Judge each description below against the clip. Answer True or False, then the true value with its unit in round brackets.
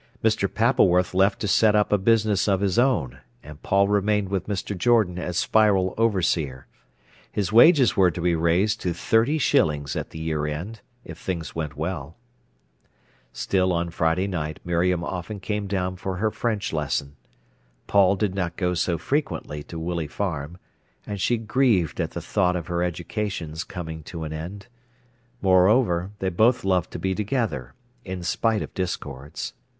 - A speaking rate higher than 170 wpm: False (165 wpm)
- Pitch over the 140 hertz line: False (95 Hz)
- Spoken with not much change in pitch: False (3.7 semitones)